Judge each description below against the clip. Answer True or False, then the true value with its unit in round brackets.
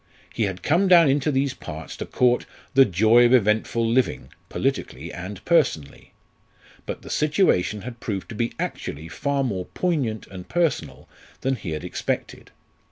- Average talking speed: True (160 wpm)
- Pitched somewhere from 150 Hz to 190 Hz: False (115 Hz)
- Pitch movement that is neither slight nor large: False (6.7 semitones)